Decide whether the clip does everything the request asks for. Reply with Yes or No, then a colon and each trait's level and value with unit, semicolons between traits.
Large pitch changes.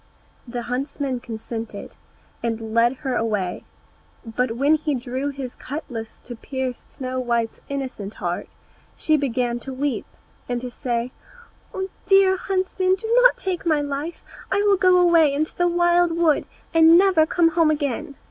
Yes: wide, 5.8 semitones